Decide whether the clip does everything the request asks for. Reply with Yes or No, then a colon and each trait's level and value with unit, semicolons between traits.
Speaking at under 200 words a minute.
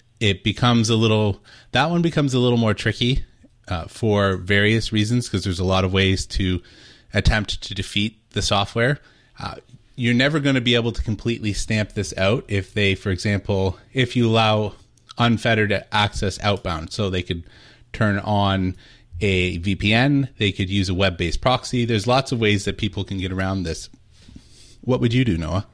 Yes: average, 180 wpm